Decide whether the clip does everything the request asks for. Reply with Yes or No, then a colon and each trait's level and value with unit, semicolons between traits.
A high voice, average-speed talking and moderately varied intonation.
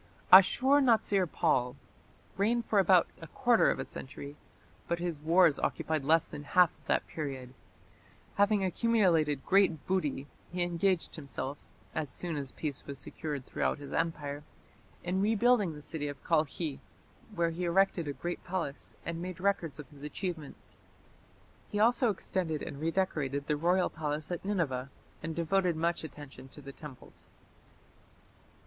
No: medium, 165 Hz; average, 150 wpm; average, 4.3 semitones